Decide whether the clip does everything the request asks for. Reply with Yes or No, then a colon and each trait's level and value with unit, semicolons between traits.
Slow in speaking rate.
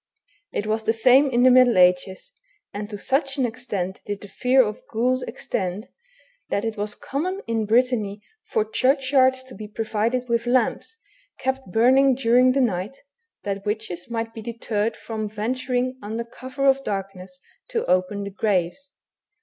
No: average, 160 wpm